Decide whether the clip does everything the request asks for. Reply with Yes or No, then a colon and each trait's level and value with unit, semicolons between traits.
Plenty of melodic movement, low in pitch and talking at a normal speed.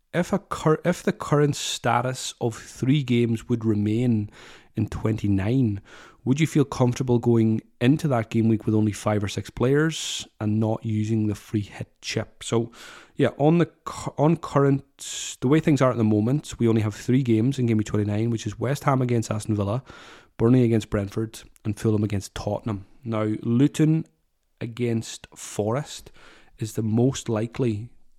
No: average, 3.7 semitones; low, 115 Hz; average, 175 wpm